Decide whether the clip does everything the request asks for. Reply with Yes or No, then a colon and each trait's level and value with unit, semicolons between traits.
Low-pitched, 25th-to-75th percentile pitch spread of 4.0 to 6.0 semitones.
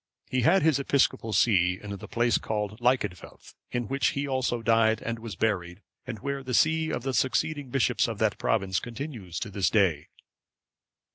Yes: low, 115 Hz; average, 4.3 semitones